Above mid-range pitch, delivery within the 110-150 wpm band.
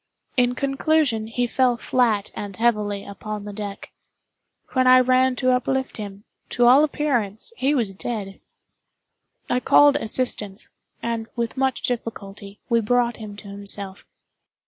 Yes: high, 235 Hz; average, 140 wpm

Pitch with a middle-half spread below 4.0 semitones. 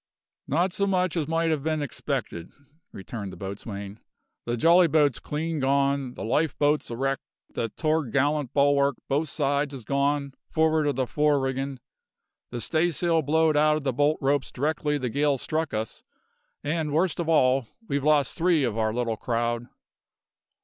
Yes: average, 3.4 semitones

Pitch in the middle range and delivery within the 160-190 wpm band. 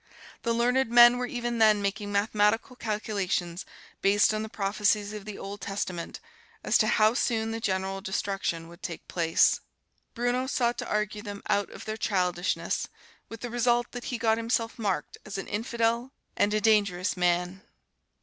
No: high, 210 Hz; average, 170 wpm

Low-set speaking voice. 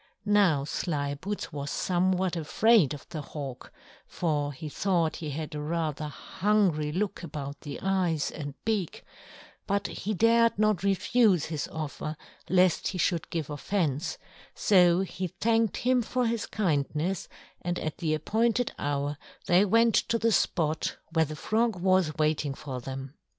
No: medium, 170 Hz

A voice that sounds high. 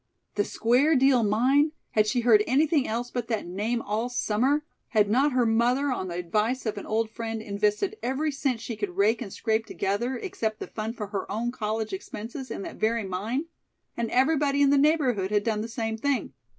Yes: high, 230 Hz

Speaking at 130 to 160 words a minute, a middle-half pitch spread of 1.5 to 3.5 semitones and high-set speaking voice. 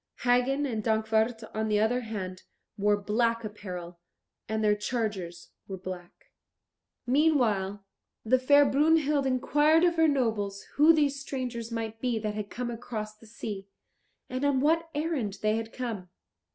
No: average, 150 wpm; average, 4.6 semitones; high, 225 Hz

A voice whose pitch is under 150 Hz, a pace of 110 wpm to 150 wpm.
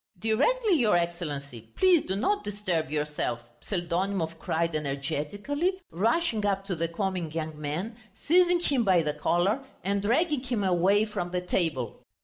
No: medium, 185 Hz; average, 145 wpm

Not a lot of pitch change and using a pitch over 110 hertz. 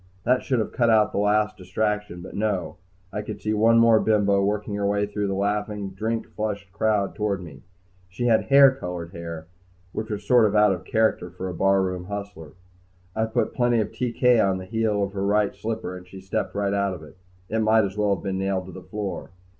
No: narrow, 2.3 semitones; low, 100 Hz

